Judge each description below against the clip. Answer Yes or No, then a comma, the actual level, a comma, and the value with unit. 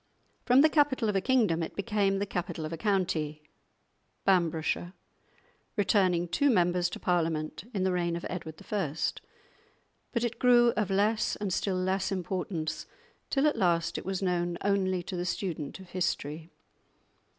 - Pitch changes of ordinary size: Yes, average, 3.1 semitones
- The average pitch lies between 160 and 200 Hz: Yes, medium, 185 Hz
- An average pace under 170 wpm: Yes, average, 160 wpm